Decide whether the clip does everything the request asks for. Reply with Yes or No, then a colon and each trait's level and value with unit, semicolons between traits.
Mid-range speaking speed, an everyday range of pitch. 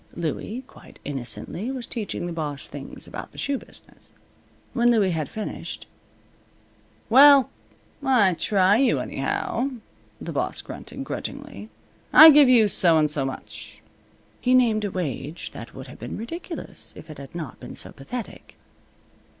No: average, 150 wpm; wide, 8.5 semitones